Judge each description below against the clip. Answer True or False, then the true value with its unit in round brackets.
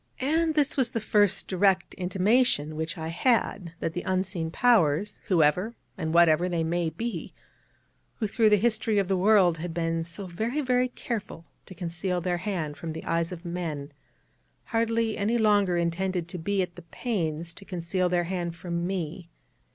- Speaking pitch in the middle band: True (180 Hz)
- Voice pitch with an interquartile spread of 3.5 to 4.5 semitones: True (3.9 semitones)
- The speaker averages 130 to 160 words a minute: False (175 wpm)